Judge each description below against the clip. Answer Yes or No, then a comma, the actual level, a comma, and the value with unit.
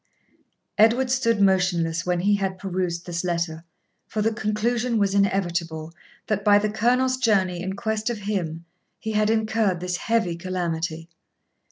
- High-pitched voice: Yes, high, 195 Hz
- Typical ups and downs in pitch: Yes, average, 3.9 semitones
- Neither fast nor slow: Yes, average, 150 wpm